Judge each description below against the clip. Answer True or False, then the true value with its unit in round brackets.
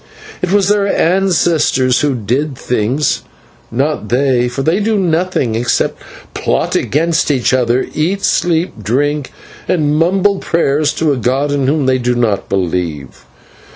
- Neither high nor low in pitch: True (145 Hz)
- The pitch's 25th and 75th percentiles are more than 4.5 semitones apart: True (5.3 semitones)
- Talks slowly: False (150 wpm)